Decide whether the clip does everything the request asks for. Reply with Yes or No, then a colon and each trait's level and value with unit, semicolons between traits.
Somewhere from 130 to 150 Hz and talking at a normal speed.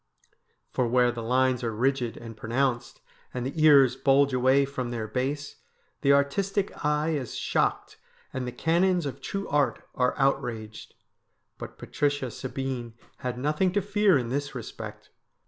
Yes: low, 135 Hz; average, 150 wpm